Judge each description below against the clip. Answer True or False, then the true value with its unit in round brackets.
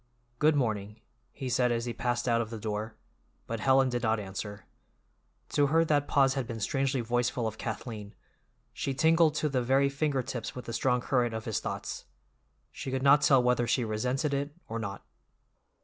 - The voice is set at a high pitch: False (125 Hz)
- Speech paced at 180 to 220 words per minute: True (190 wpm)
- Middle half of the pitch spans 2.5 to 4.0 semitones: True (3.4 semitones)